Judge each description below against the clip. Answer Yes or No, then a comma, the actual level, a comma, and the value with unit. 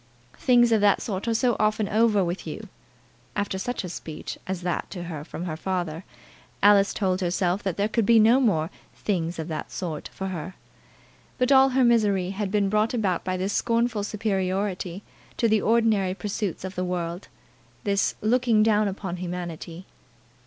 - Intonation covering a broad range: No, average, 3.3 semitones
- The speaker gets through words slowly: No, average, 175 wpm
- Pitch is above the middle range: Yes, high, 195 Hz